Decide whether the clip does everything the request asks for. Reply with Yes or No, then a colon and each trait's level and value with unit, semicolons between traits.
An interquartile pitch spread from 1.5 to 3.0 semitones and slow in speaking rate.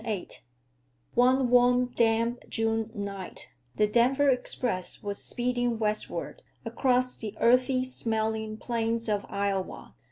Yes: narrow, 2.6 semitones; slow, 115 wpm